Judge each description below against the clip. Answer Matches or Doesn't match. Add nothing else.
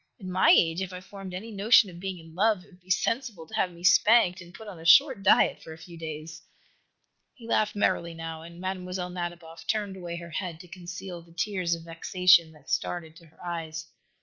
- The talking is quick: Matches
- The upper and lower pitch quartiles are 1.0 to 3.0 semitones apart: Matches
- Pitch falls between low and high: Matches